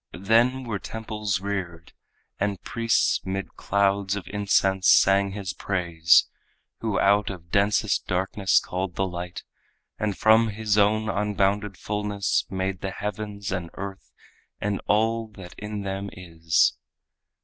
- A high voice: No, low, 100 Hz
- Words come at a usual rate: No, slow, 130 wpm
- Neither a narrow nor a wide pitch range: No, narrow, 1.7 semitones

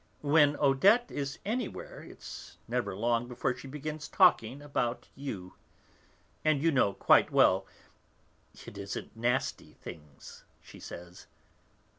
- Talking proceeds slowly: Yes, slow, 120 wpm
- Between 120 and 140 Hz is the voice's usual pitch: Yes, low, 135 Hz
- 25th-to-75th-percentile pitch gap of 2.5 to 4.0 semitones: No, average, 4.6 semitones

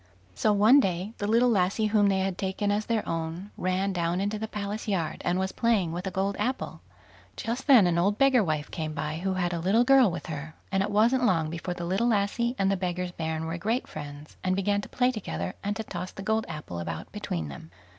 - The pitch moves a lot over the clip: No, average, 4.1 semitones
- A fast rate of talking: Yes, fast, 235 wpm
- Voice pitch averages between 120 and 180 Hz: No, high, 195 Hz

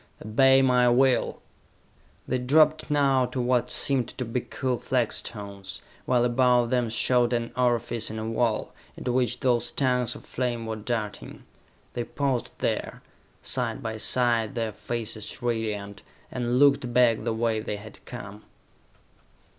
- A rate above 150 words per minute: No, average, 145 wpm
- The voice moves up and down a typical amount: No, narrow, 2.1 semitones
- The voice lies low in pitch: Yes, low, 120 Hz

